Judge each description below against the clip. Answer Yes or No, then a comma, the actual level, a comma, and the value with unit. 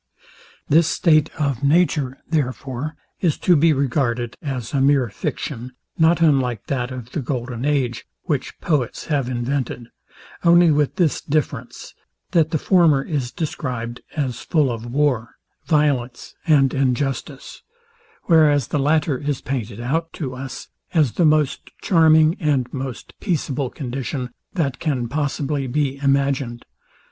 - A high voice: No, medium, 140 Hz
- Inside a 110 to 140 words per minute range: Yes, slow, 135 wpm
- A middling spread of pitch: Yes, average, 3.4 semitones